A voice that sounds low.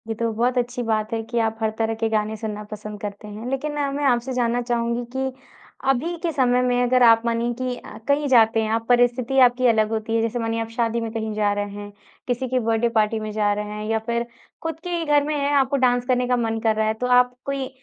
No: high, 235 Hz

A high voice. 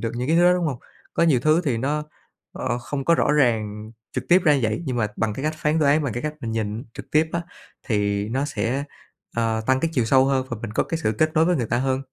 No: low, 130 Hz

